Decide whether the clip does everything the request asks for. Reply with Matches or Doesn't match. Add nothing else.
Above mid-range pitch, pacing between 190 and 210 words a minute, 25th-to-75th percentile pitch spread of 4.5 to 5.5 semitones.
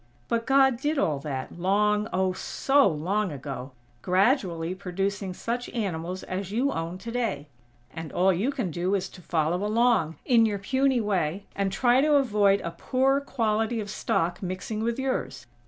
Doesn't match